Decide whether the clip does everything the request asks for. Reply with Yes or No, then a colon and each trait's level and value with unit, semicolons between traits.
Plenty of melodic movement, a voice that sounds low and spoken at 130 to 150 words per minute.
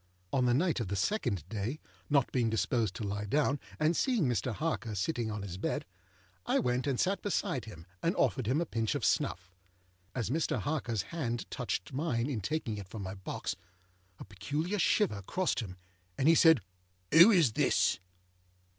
No: wide, 7.0 semitones; low, 125 Hz; average, 180 wpm